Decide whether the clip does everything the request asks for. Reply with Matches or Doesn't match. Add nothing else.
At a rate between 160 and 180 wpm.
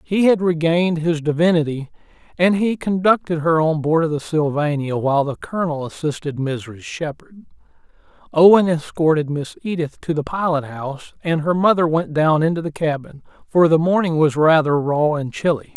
Matches